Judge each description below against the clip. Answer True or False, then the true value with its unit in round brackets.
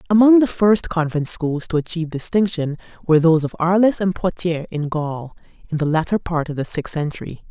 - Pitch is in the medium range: True (170 Hz)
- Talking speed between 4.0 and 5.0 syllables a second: False (5.4 syllables/s)